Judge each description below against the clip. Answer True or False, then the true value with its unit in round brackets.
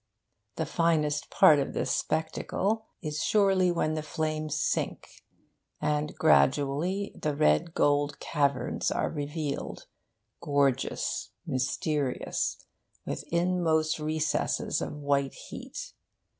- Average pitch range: False (2.2 semitones)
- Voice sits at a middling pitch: True (155 Hz)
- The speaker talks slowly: True (100 wpm)